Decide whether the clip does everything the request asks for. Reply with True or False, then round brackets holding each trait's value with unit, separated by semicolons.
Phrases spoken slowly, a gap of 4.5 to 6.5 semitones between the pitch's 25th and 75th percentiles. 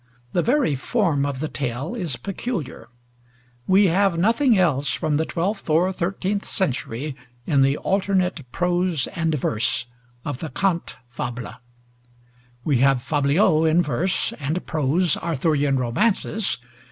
True (130 wpm; 5.2 semitones)